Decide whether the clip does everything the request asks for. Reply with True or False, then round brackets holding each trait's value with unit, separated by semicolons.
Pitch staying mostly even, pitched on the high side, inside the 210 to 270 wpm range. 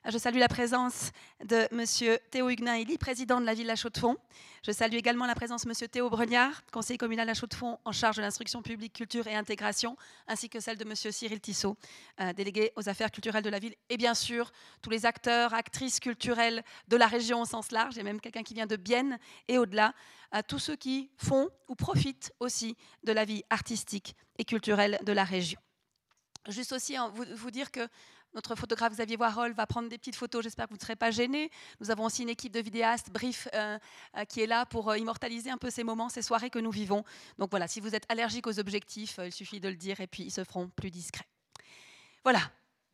True (1.9 semitones; 230 Hz; 220 wpm)